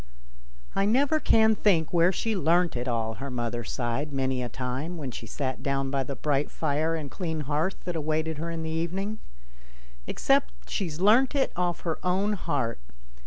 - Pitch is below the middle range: No, medium, 155 Hz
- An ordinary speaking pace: Yes, average, 185 wpm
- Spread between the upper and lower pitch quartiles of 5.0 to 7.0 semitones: Yes, wide, 5.4 semitones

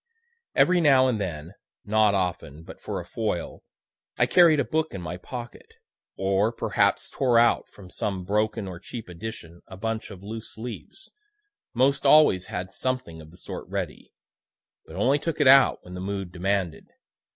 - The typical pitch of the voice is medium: No, low, 105 Hz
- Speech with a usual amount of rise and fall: No, wide, 5.7 semitones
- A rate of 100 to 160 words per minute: No, average, 170 wpm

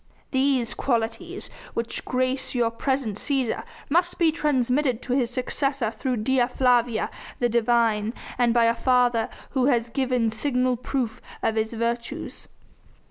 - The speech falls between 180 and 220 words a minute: No, slow, 135 wpm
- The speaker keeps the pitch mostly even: Yes, narrow, 2.3 semitones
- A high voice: Yes, high, 245 Hz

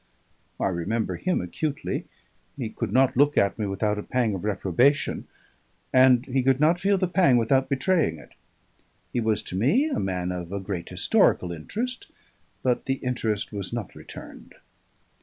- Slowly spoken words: No, average, 165 wpm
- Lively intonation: Yes, wide, 6.0 semitones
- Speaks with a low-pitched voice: Yes, low, 120 Hz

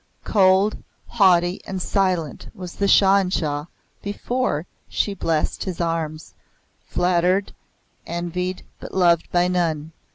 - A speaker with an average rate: No, slow, 120 wpm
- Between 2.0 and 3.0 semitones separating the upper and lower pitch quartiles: Yes, narrow, 2.4 semitones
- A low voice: No, medium, 180 Hz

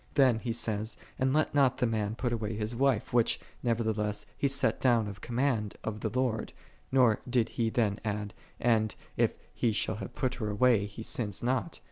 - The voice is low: Yes, low, 115 Hz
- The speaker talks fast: No, average, 190 wpm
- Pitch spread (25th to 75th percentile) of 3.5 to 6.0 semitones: No, average, 2.8 semitones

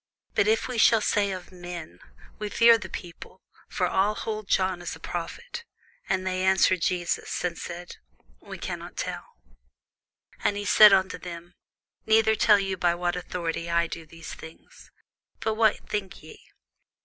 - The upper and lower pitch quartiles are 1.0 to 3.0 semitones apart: No, average, 3.4 semitones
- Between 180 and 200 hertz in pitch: Yes, medium, 185 Hz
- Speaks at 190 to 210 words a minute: No, average, 165 wpm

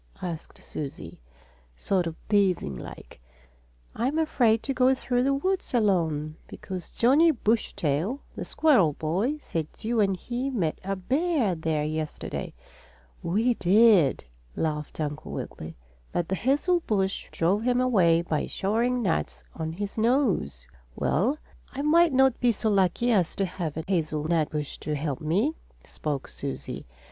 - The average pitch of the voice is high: Yes, high, 195 Hz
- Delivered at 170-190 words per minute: No, average, 145 wpm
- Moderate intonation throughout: No, wide, 7.8 semitones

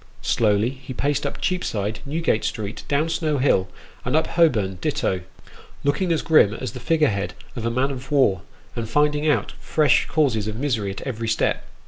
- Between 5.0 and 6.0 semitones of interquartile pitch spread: Yes, wide, 5.4 semitones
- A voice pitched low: Yes, low, 130 Hz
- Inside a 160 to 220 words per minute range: Yes, average, 180 wpm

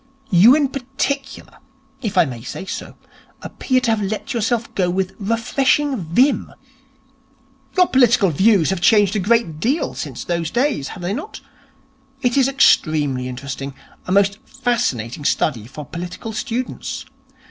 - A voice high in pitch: Yes, high, 210 Hz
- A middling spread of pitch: No, wide, 7.0 semitones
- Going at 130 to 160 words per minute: Yes, average, 145 wpm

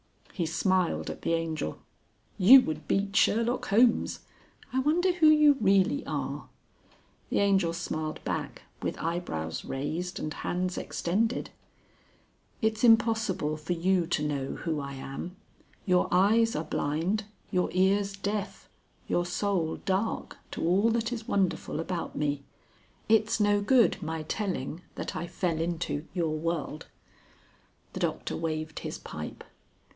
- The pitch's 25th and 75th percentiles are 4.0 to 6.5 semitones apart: Yes, average, 5.0 semitones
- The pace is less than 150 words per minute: Yes, slow, 135 wpm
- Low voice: No, medium, 180 Hz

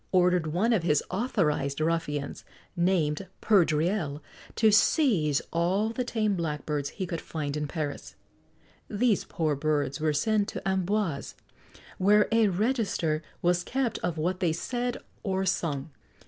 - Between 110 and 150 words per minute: Yes, slow, 135 wpm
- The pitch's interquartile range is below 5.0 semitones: No, average, 5.3 semitones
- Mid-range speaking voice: Yes, medium, 175 Hz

